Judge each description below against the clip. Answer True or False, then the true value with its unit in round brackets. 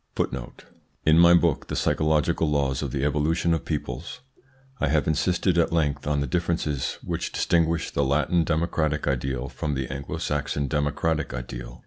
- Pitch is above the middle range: False (75 Hz)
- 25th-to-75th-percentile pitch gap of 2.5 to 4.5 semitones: True (2.9 semitones)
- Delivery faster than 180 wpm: False (155 wpm)